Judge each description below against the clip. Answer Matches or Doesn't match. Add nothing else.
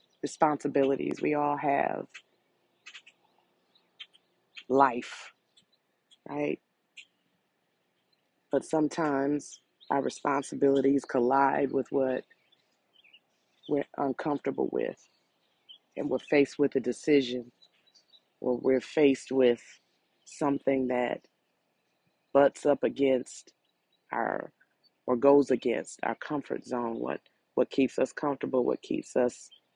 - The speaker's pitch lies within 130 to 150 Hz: Matches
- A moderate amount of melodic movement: Doesn't match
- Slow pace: Matches